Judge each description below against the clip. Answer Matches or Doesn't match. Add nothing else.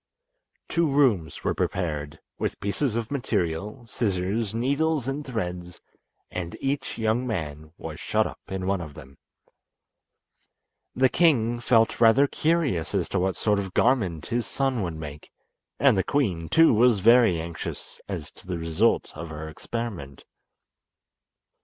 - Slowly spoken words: Doesn't match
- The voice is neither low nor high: Doesn't match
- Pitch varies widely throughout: Matches